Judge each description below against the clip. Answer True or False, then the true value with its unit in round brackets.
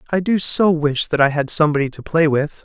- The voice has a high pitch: False (155 Hz)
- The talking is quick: True (250 wpm)